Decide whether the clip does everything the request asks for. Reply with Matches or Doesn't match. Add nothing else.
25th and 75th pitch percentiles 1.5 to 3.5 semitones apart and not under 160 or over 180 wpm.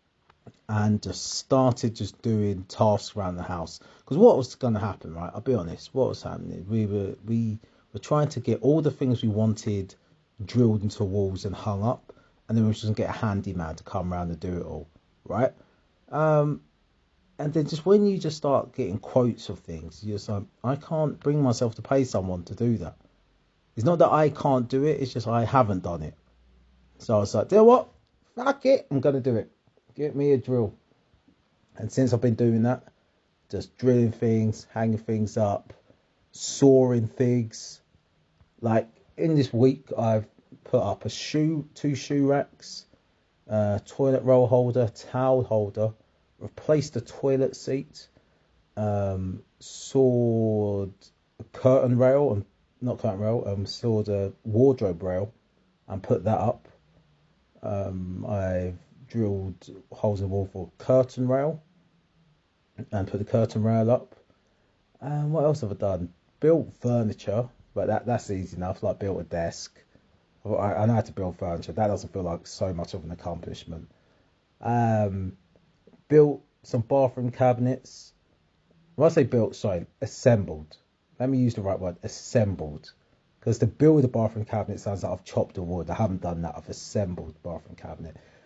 Doesn't match